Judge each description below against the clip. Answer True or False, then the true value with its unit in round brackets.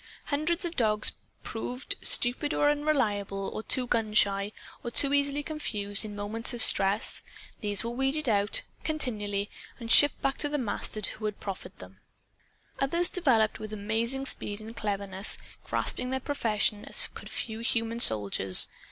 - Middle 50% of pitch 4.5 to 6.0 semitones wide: True (4.8 semitones)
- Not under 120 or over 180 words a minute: True (150 wpm)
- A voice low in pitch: False (225 Hz)